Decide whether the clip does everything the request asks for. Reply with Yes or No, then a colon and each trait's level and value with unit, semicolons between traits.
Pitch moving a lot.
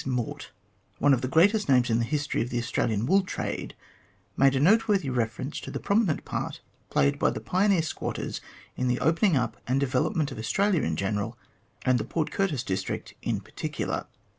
Yes: wide, 5.9 semitones